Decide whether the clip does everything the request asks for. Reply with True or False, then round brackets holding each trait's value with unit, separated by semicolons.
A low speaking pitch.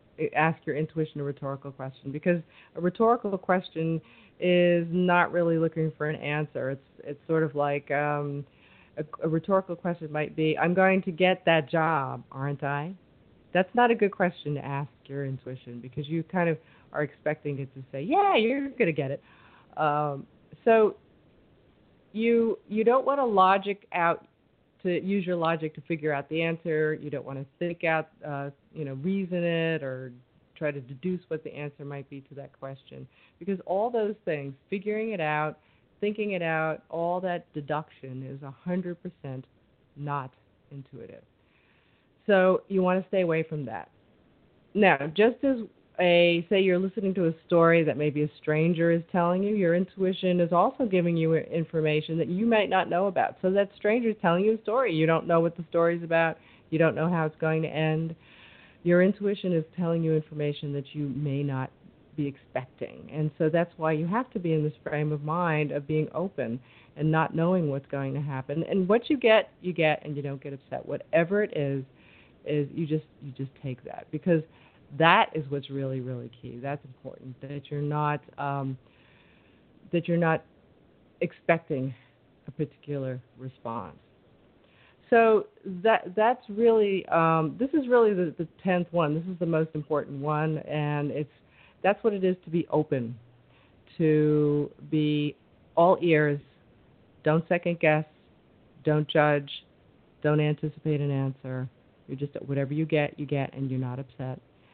False (155 Hz)